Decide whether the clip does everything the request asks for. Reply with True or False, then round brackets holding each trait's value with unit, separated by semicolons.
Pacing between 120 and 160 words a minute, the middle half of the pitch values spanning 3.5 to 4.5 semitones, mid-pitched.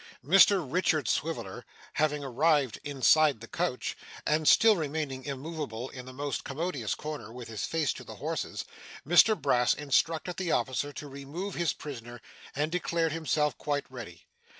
True (150 wpm; 3.9 semitones; 145 Hz)